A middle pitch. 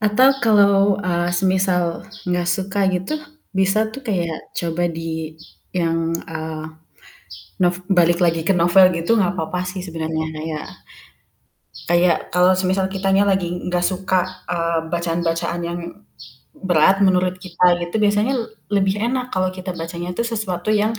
Yes: medium, 180 Hz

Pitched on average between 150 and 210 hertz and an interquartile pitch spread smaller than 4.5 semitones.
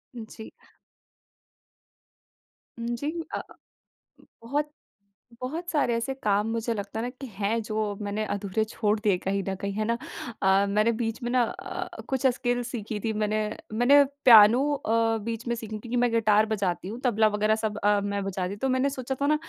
No: high, 220 Hz; average, 2.8 semitones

